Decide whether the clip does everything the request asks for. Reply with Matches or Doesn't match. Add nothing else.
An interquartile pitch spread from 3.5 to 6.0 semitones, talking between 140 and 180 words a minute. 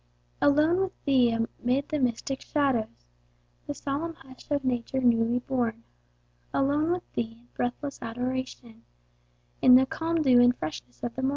Doesn't match